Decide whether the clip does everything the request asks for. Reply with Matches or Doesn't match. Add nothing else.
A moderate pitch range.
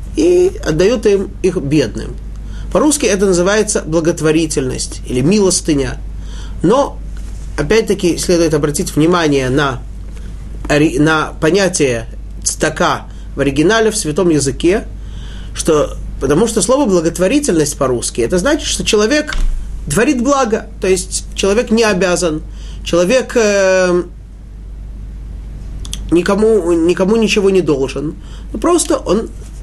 Doesn't match